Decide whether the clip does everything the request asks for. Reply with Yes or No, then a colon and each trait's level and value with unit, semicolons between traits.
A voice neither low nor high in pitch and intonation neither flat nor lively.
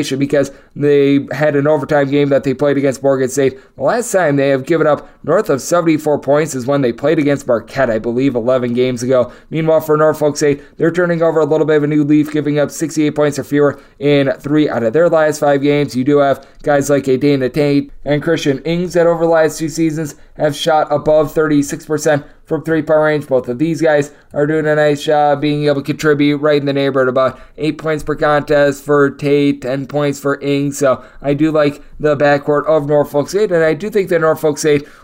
No: medium, 145 Hz; narrow, 1.6 semitones